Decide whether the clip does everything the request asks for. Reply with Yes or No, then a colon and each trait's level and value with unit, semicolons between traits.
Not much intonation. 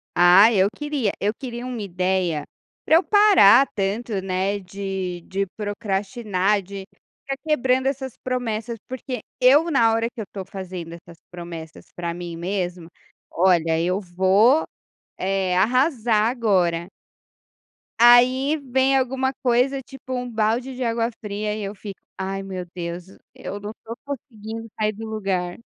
No: average, 4.9 semitones